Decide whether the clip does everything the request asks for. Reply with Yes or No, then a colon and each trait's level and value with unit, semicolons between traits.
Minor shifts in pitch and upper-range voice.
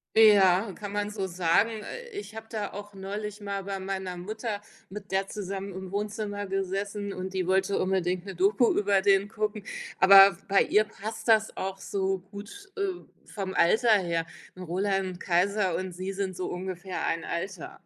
Yes: narrow, 1.7 semitones; high, 195 Hz